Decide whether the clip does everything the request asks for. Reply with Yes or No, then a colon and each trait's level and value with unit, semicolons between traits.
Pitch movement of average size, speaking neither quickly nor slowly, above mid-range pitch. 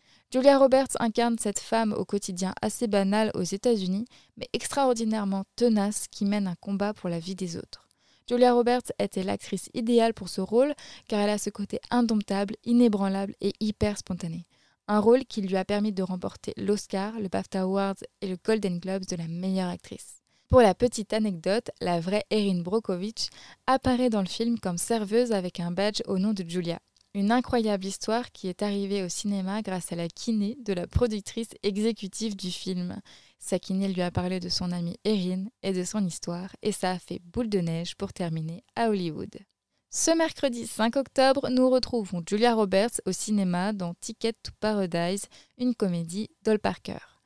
Yes: average, 3.4 semitones; average, 180 wpm; high, 205 Hz